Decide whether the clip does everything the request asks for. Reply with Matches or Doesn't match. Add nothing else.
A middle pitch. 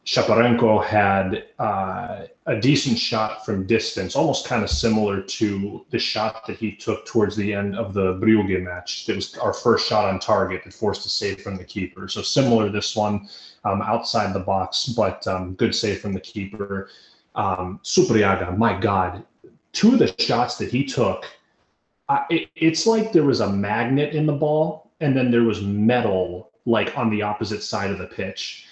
Doesn't match